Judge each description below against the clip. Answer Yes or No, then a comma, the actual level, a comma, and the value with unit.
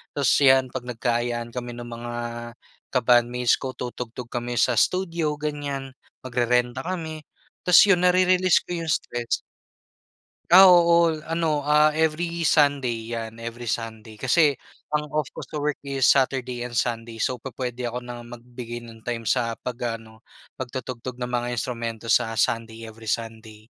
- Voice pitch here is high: No, low, 125 Hz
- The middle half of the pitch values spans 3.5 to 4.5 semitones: Yes, average, 3.9 semitones